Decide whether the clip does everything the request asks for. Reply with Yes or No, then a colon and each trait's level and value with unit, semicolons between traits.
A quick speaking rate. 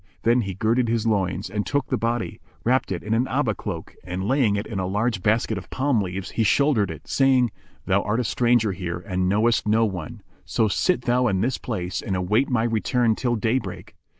Yes: fast, 215 wpm